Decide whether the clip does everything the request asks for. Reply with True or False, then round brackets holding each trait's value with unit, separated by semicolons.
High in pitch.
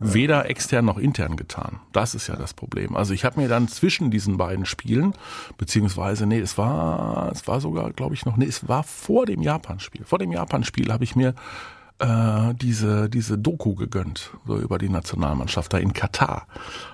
False (115 Hz)